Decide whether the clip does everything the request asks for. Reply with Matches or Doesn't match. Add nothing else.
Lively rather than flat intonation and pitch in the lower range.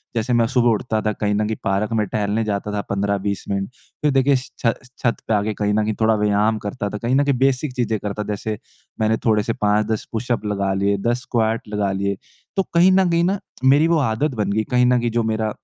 Doesn't match